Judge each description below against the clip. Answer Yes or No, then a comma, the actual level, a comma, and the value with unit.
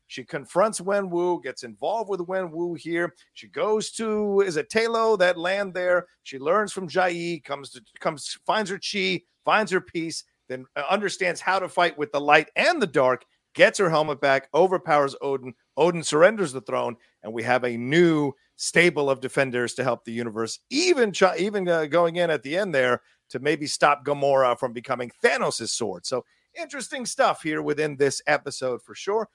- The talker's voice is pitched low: No, medium, 165 Hz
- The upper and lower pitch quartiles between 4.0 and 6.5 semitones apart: Yes, wide, 5.5 semitones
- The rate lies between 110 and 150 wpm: No, average, 180 wpm